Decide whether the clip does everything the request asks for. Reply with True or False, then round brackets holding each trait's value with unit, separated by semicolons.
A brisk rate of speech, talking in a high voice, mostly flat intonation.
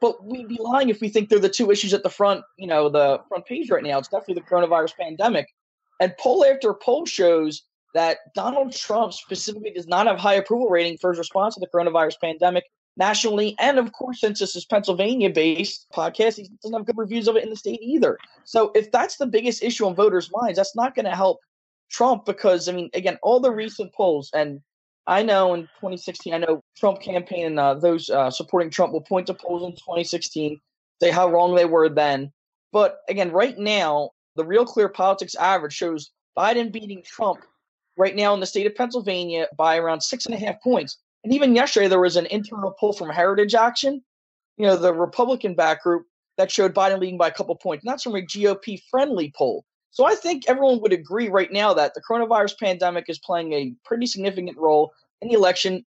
False (210 wpm; 195 Hz; 4.6 semitones)